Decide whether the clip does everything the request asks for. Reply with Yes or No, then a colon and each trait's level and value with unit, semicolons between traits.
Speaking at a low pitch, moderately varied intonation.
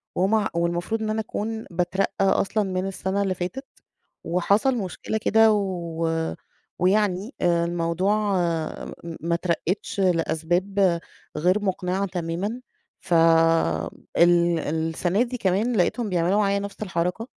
No: medium, 185 Hz; average, 3.3 semitones